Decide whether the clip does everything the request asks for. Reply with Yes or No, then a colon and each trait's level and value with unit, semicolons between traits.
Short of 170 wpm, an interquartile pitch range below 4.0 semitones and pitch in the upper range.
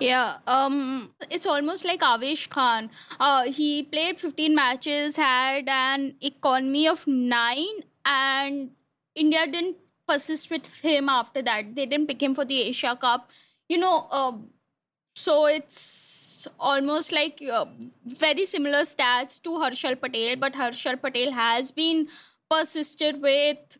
Yes: slow, 135 wpm; average, 3.3 semitones; very high, 280 Hz